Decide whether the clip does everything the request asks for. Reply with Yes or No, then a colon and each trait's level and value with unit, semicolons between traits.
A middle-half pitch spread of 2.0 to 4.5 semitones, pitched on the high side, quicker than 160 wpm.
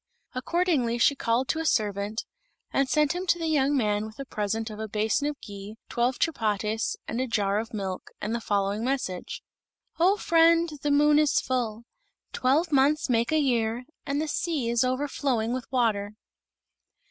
No: average, 5.1 semitones; high, 245 Hz; average, 170 wpm